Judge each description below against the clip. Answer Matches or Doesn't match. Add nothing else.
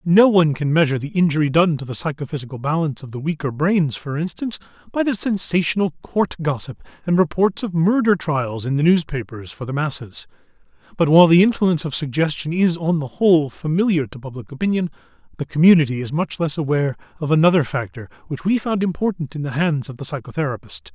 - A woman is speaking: Doesn't match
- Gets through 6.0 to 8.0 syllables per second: Matches